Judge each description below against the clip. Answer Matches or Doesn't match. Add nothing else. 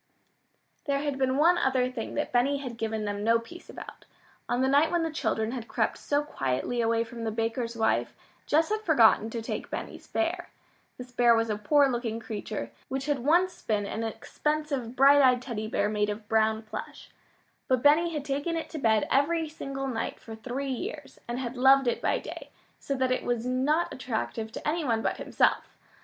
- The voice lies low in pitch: Doesn't match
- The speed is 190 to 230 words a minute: Matches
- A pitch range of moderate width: Matches